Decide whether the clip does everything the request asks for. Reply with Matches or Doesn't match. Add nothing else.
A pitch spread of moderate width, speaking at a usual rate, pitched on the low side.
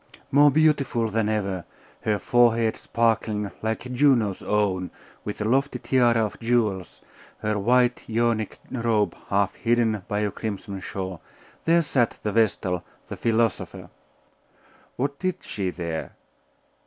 Doesn't match